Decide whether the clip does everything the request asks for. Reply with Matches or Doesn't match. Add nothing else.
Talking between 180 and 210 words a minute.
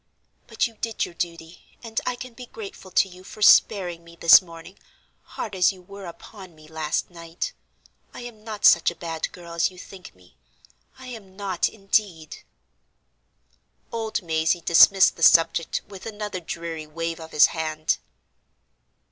Doesn't match